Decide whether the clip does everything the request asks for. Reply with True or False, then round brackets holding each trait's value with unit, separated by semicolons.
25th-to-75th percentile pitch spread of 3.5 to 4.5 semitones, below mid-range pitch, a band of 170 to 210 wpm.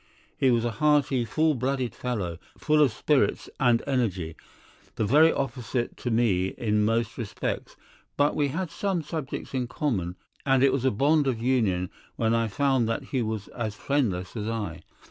True (4.1 semitones; 120 Hz; 175 wpm)